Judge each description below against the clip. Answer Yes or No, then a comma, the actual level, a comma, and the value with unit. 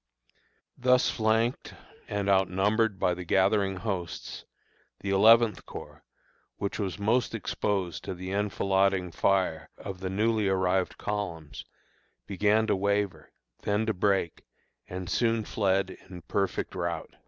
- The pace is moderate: No, slow, 125 wpm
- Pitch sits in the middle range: No, low, 100 Hz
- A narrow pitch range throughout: Yes, narrow, 2.2 semitones